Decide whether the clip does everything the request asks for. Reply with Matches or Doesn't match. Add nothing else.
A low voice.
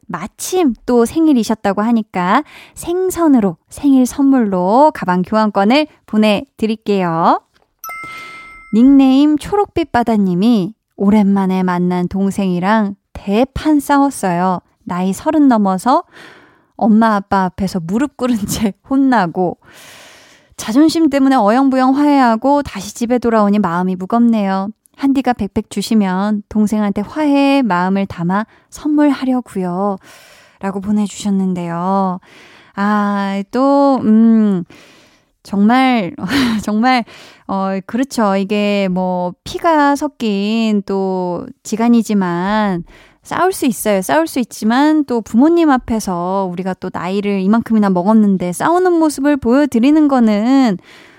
Doesn't match